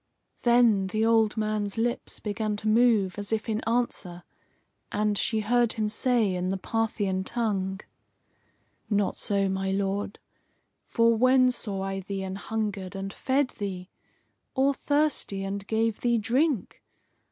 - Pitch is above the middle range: Yes, high, 215 Hz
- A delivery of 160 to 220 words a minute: No, average, 140 wpm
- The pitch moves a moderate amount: Yes, average, 3.0 semitones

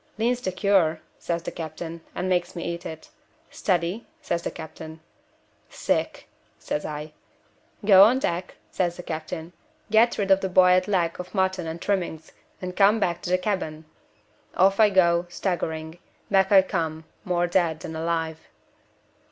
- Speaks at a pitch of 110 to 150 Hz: No, medium, 175 Hz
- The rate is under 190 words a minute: Yes, average, 160 wpm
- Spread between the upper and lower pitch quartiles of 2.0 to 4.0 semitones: Yes, average, 2.8 semitones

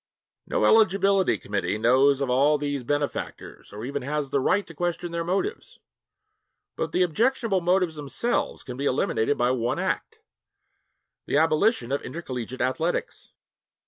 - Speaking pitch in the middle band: Yes, medium, 145 Hz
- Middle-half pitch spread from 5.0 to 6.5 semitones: Yes, wide, 5.6 semitones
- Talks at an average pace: Yes, average, 145 wpm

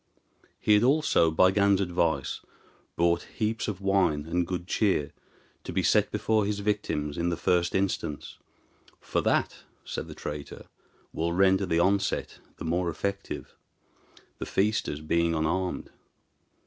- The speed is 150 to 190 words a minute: No, average, 140 wpm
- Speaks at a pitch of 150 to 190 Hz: No, very low, 90 Hz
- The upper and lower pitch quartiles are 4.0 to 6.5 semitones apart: No, average, 3.2 semitones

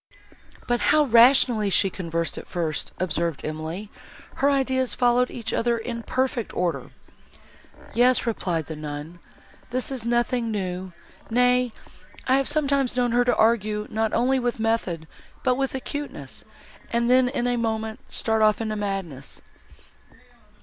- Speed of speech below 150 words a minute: Yes, average, 140 wpm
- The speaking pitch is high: Yes, high, 230 Hz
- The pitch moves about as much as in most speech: Yes, average, 4.8 semitones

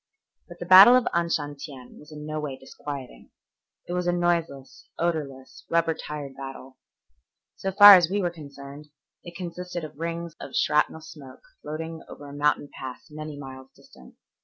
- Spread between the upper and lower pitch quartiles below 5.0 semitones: Yes, average, 3.5 semitones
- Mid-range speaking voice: Yes, medium, 155 Hz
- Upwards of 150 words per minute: Yes, average, 160 wpm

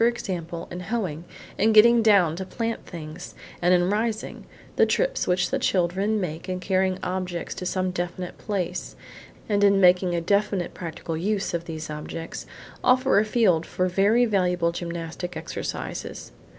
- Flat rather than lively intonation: No, average, 3.3 semitones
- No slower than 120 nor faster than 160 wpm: Yes, average, 150 wpm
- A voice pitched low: No, medium, 185 Hz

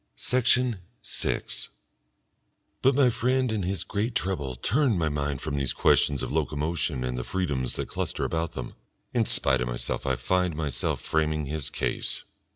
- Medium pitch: No, very low, 80 Hz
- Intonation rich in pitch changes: Yes, wide, 6.7 semitones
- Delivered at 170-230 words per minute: No, average, 160 wpm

